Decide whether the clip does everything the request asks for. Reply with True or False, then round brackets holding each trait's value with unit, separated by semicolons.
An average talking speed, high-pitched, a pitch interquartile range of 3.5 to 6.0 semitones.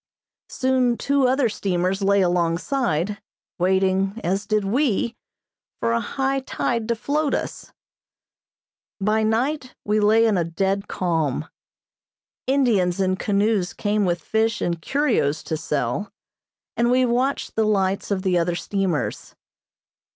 False (130 wpm; 205 Hz; 4.7 semitones)